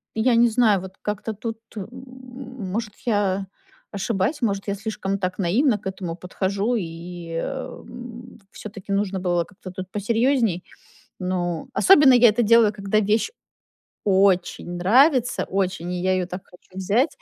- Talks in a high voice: Yes, high, 205 Hz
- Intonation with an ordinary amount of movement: Yes, average, 4.0 semitones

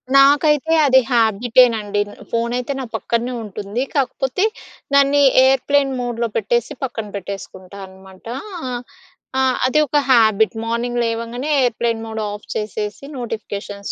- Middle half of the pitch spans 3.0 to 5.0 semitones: Yes, average, 3.5 semitones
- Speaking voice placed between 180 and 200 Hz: No, high, 235 Hz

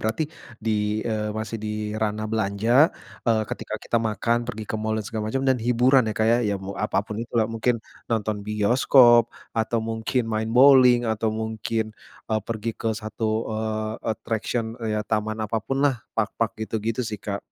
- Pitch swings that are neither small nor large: No, narrow, 1.4 semitones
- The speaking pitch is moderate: No, low, 110 Hz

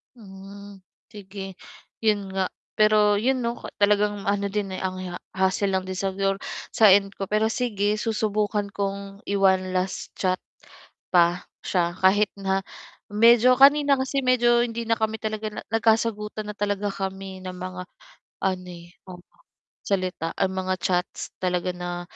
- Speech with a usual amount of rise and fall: No, narrow, 2.3 semitones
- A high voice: Yes, high, 200 Hz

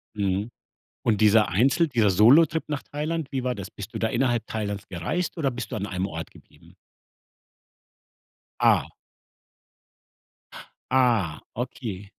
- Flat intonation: No, average, 5.0 semitones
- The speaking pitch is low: Yes, low, 115 Hz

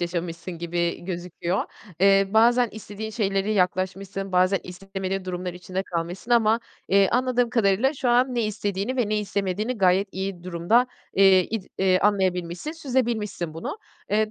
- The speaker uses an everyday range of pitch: Yes, average, 3.2 semitones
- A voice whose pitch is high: Yes, high, 195 Hz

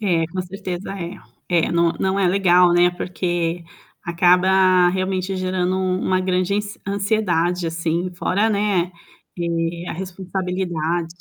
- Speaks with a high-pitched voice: No, medium, 180 Hz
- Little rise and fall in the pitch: Yes, narrow, 1.5 semitones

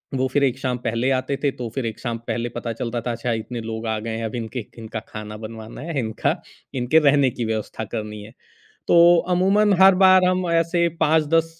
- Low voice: Yes, low, 125 Hz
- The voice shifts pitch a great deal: Yes, wide, 6.0 semitones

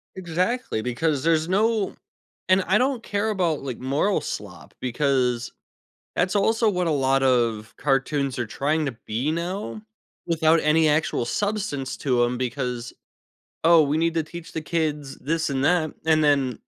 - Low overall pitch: No, medium, 155 Hz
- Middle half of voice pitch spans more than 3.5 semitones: Yes, average, 5.2 semitones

